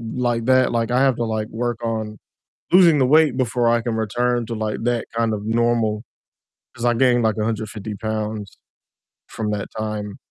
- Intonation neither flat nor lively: No, narrow, 2.0 semitones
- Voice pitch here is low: Yes, low, 115 Hz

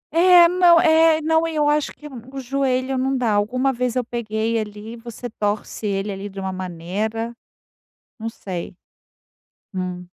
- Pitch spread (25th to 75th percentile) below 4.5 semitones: No, average, 5.2 semitones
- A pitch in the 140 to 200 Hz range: No, high, 235 Hz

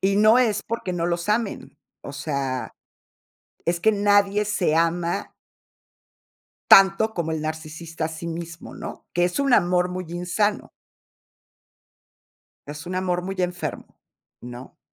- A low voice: No, medium, 175 Hz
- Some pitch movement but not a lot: Yes, average, 3.6 semitones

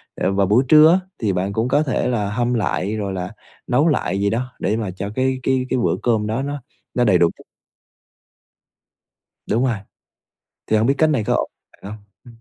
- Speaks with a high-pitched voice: No, low, 115 Hz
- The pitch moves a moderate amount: Yes, average, 4.3 semitones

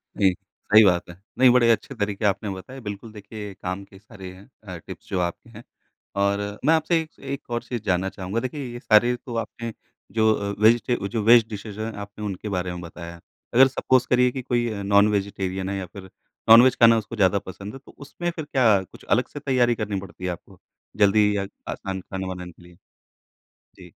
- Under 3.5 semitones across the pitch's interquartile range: No, average, 3.9 semitones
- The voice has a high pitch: No, low, 105 Hz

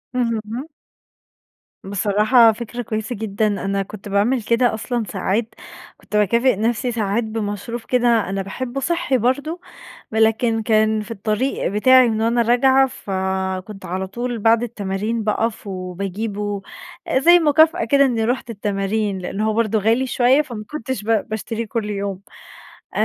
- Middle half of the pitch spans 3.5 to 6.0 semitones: No, average, 3.0 semitones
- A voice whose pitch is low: No, high, 220 Hz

